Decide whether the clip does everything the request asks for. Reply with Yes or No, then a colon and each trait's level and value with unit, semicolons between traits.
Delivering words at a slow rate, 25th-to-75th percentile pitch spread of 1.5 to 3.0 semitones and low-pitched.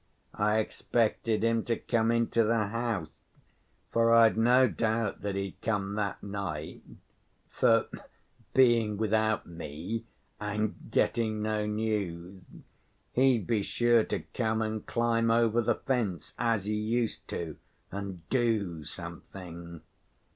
Yes: slow, 125 wpm; average, 2.7 semitones; low, 110 Hz